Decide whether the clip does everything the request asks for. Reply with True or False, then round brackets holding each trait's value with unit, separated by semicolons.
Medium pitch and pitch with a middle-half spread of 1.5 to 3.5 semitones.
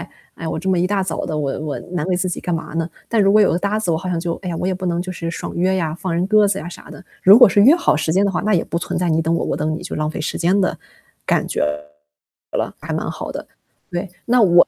True (180 Hz; 2.9 semitones)